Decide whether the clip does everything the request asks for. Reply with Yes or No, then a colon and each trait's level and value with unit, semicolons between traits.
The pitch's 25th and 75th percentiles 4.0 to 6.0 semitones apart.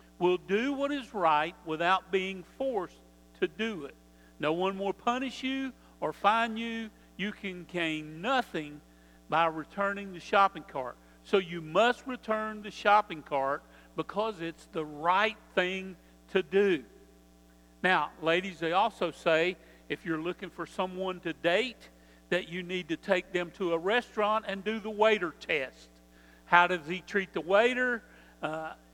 Yes: average, 4.6 semitones